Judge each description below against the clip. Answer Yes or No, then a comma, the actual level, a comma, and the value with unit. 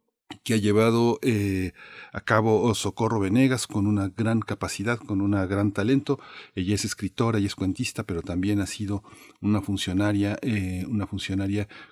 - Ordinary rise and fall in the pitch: No, narrow, 2.3 semitones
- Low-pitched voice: Yes, low, 105 Hz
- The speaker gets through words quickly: No, average, 155 wpm